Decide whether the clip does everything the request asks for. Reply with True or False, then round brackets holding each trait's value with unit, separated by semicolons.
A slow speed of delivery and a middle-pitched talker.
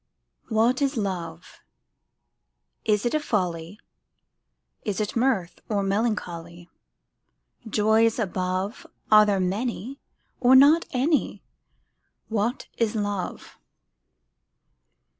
False (90 wpm; 210 Hz)